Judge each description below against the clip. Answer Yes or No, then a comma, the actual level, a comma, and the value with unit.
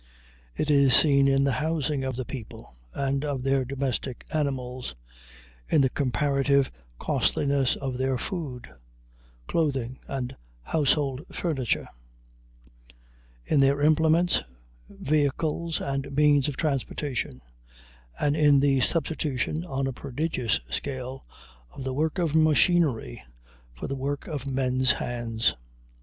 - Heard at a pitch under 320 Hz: Yes, medium, 140 Hz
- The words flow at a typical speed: No, slow, 120 wpm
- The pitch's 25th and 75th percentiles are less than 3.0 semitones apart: Yes, narrow, 2.4 semitones